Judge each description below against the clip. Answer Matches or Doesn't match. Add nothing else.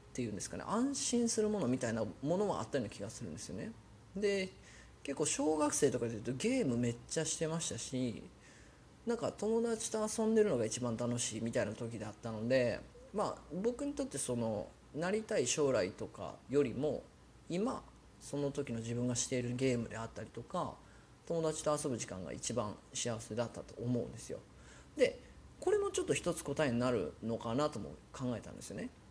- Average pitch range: Doesn't match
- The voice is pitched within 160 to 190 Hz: Doesn't match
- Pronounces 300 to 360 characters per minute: Doesn't match